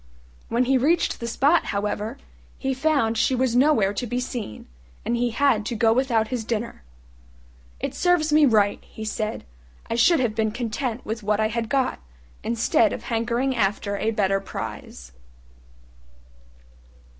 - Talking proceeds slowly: No, average, 155 wpm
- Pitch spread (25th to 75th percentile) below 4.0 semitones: Yes, average, 3.2 semitones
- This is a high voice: Yes, high, 235 Hz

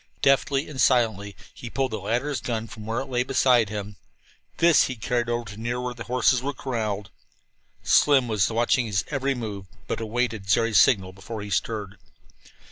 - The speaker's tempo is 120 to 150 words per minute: No, average, 185 wpm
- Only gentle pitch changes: No, average, 3.2 semitones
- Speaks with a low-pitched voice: Yes, low, 120 Hz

